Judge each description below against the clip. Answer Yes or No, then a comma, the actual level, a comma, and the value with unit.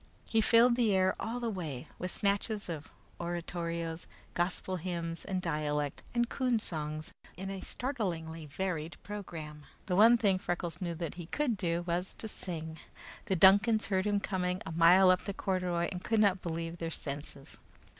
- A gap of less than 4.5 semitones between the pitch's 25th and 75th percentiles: Yes, average, 3.3 semitones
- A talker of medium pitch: Yes, medium, 180 Hz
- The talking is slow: No, average, 170 wpm